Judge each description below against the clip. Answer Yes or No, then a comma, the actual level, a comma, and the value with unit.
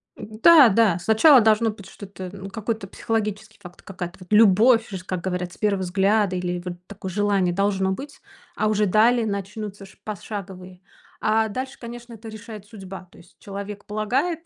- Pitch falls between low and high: No, high, 205 Hz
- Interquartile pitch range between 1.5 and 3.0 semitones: Yes, narrow, 2.6 semitones